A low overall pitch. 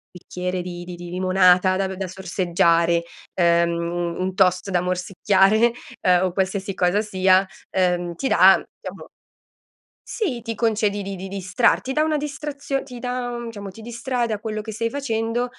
No: high, 195 Hz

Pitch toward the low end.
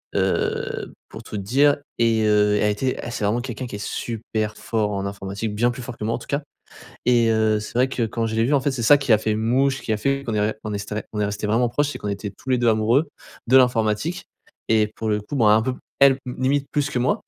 Yes: low, 115 Hz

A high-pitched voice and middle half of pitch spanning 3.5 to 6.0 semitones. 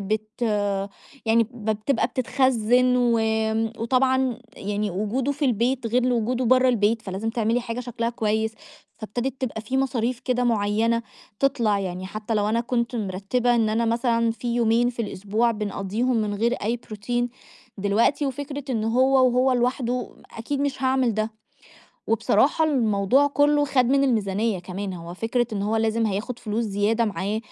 No: high, 230 Hz; average, 2.8 semitones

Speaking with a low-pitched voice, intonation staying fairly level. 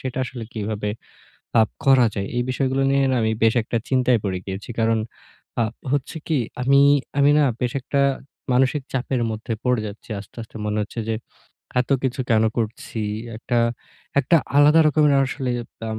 No: low, 125 Hz; average, 3.5 semitones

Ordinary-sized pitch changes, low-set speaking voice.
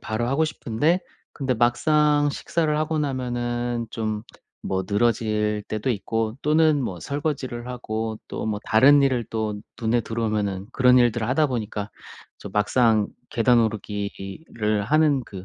Yes: average, 4.0 semitones; low, 120 Hz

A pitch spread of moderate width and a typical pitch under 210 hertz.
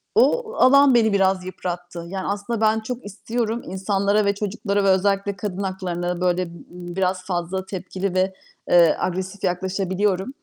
No: narrow, 2.0 semitones; high, 190 Hz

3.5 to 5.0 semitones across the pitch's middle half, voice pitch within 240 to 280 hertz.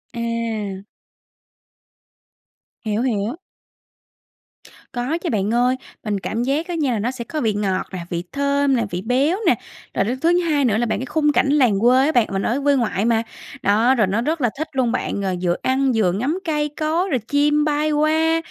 No: wide, 5.5 semitones; very high, 250 Hz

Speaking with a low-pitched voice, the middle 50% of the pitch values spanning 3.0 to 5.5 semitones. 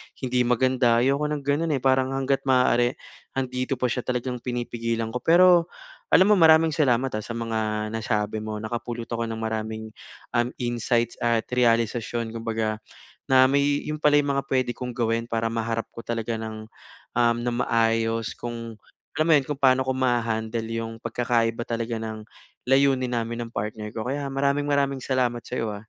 No: low, 120 Hz; narrow, 2.5 semitones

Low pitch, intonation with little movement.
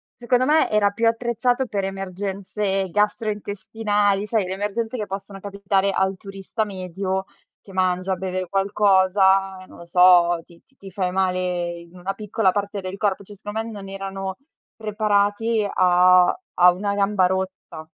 No: high, 195 Hz; narrow, 1.8 semitones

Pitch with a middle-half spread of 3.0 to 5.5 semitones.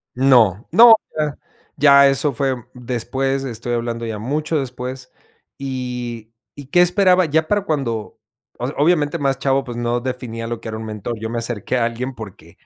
Yes: average, 3.3 semitones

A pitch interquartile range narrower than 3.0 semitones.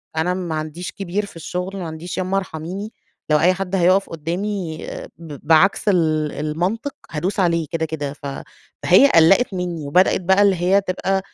No: average, 3.3 semitones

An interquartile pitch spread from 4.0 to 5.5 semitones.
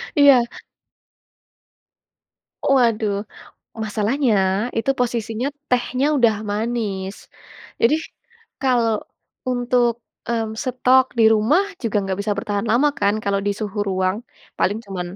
No: average, 3.3 semitones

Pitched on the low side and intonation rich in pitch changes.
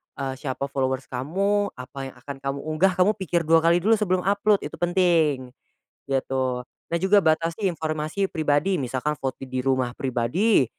No: medium, 155 Hz; wide, 5.7 semitones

